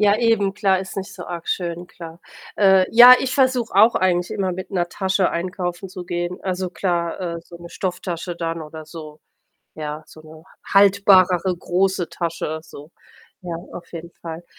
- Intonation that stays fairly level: Yes, narrow, 2.3 semitones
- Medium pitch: Yes, medium, 180 Hz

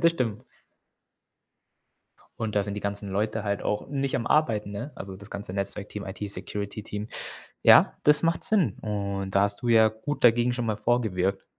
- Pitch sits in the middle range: No, low, 105 Hz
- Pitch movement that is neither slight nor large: Yes, average, 3.1 semitones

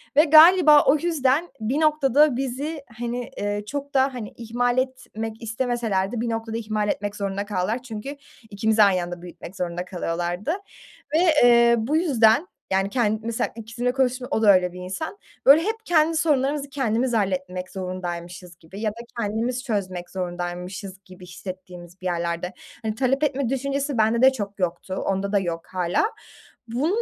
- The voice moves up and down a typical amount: No, wide, 6.0 semitones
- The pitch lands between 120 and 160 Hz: No, high, 225 Hz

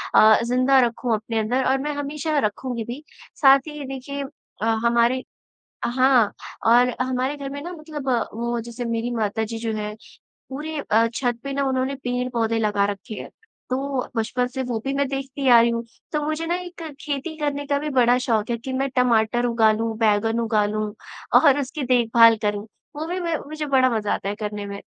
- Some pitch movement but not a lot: Yes, average, 3.5 semitones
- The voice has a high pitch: Yes, very high, 250 Hz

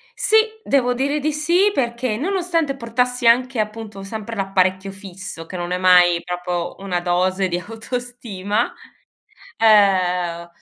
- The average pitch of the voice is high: Yes, high, 210 Hz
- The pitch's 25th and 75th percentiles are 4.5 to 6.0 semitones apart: Yes, wide, 5.4 semitones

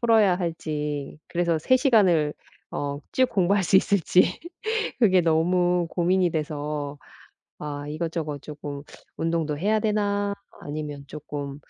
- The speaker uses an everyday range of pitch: Yes, average, 4.2 semitones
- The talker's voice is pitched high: No, medium, 165 Hz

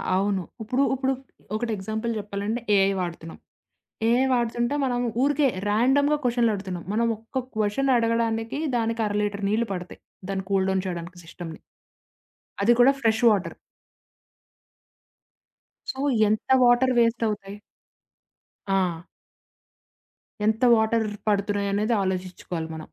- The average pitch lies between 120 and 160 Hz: No, high, 220 Hz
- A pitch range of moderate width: Yes, average, 3.4 semitones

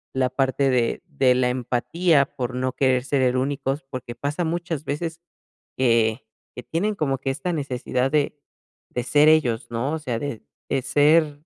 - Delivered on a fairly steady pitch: No, average, 3.0 semitones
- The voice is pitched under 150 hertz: Yes, low, 135 Hz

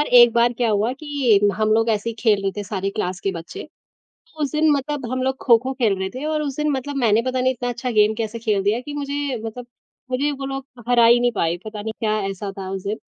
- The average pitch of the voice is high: Yes, high, 235 Hz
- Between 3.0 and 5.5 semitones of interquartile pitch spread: Yes, average, 4.0 semitones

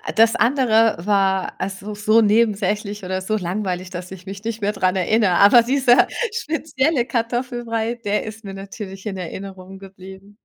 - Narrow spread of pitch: No, average, 3.1 semitones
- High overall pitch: Yes, high, 205 Hz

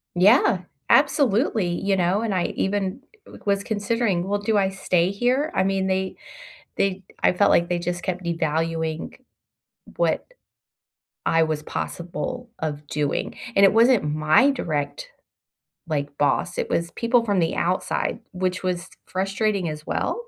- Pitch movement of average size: Yes, average, 3.5 semitones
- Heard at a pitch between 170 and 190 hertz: Yes, medium, 185 Hz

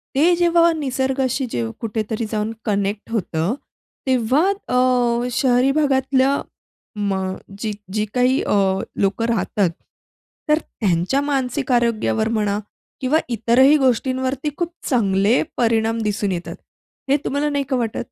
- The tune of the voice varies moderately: Yes, average, 3.9 semitones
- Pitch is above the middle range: Yes, high, 245 Hz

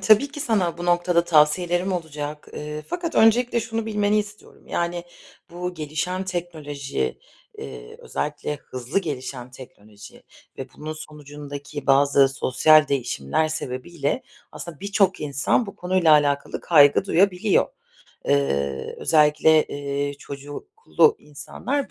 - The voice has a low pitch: No, medium, 155 Hz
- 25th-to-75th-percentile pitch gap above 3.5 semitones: Yes, average, 4.4 semitones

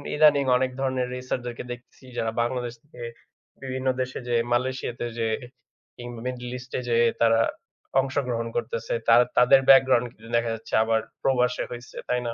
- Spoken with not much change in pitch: Yes, narrow, 1.8 semitones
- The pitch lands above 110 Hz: Yes, low, 125 Hz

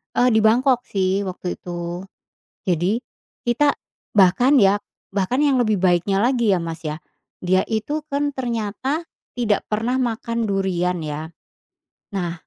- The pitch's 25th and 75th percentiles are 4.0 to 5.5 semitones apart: Yes, average, 5.2 semitones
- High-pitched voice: Yes, high, 205 Hz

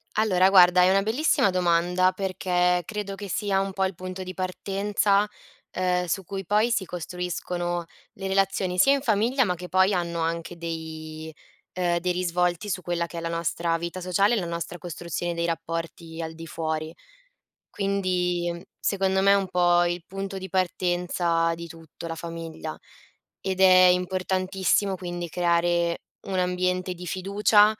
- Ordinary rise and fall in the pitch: No, narrow, 2.0 semitones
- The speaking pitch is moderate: Yes, medium, 180 Hz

